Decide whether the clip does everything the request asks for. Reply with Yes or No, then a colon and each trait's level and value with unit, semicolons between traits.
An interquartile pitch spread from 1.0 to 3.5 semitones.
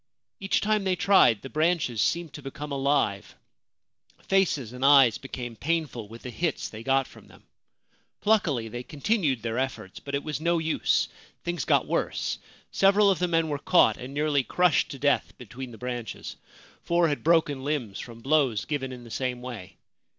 No: average, 5.2 semitones